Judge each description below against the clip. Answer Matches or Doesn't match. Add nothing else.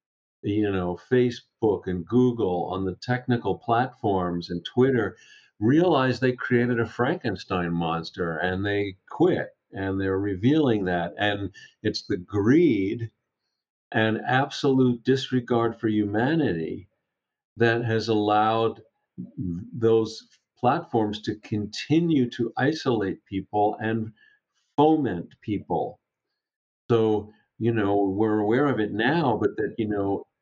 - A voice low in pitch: Matches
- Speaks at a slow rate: Matches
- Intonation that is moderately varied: Matches